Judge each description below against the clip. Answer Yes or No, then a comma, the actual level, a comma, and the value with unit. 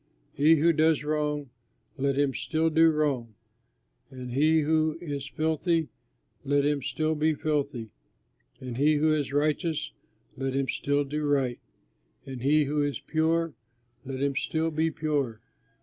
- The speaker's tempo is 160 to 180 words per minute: No, average, 150 wpm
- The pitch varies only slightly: Yes, narrow, 2.3 semitones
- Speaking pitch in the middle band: Yes, medium, 150 Hz